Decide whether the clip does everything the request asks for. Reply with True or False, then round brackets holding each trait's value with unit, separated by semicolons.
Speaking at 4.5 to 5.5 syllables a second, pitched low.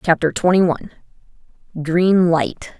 False (4.6 syllables/s; 170 Hz)